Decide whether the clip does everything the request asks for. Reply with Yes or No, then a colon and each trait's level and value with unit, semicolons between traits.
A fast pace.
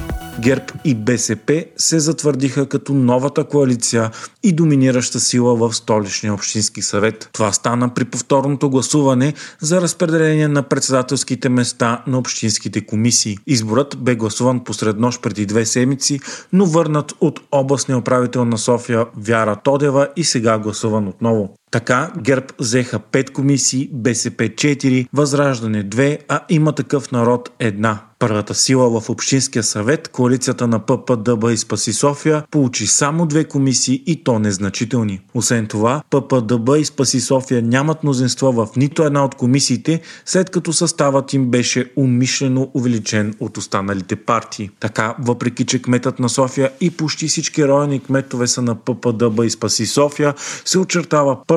No: average, 145 wpm